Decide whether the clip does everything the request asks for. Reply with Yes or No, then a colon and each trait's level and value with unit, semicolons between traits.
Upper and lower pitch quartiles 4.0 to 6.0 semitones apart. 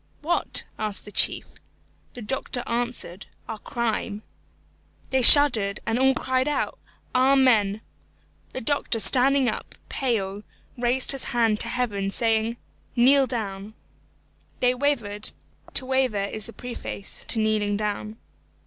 No: average, 3.5 semitones